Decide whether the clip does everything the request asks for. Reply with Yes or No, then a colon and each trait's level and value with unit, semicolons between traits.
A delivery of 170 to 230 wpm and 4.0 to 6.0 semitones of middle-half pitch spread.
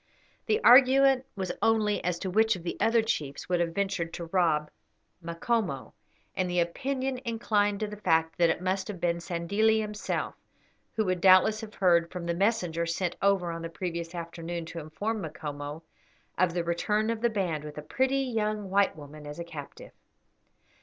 Yes: average, 180 wpm; average, 4.3 semitones